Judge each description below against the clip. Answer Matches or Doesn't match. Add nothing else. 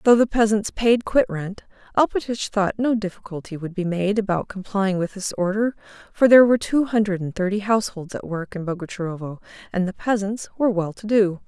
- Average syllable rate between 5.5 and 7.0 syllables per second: Matches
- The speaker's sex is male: Doesn't match